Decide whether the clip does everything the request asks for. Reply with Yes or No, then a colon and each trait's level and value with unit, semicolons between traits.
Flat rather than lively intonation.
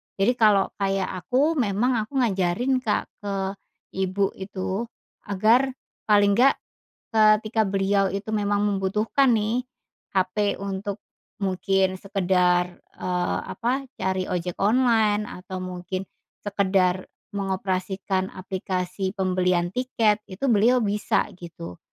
Yes: narrow, 2.2 semitones